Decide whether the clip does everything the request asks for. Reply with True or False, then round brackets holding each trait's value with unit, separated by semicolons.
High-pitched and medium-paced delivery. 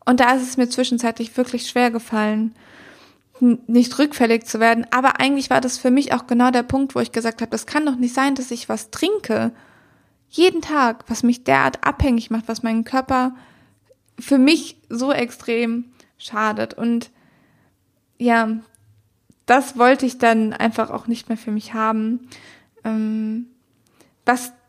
True (240 Hz; 160 wpm)